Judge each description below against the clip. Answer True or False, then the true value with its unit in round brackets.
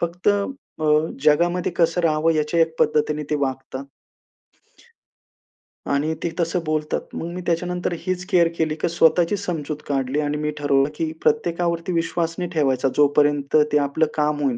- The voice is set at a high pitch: False (155 Hz)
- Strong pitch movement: False (2.6 semitones)